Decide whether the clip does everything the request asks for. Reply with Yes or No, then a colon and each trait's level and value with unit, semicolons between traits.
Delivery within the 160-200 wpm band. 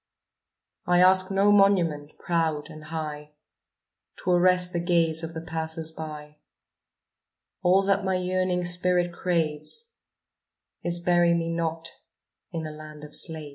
No: slow, 135 wpm